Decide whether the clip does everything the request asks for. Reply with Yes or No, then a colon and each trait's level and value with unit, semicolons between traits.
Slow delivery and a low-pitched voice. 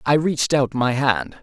No: fast, 210 wpm; low, 130 Hz